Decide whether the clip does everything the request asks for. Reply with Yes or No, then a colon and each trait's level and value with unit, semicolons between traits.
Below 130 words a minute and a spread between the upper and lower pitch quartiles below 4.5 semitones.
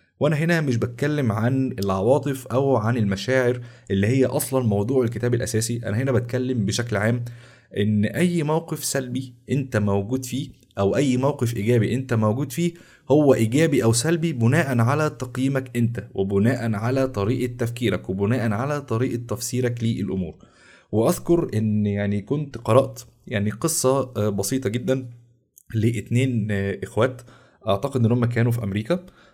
No: fast, 135 wpm; average, 3.4 semitones